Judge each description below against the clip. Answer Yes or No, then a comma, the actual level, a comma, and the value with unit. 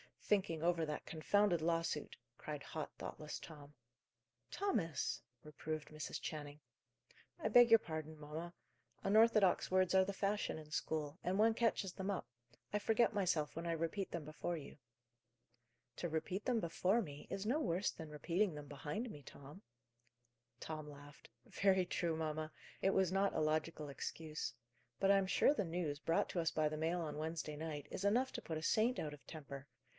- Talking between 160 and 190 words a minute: Yes, average, 175 wpm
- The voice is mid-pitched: Yes, medium, 165 Hz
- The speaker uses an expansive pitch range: No, average, 4.2 semitones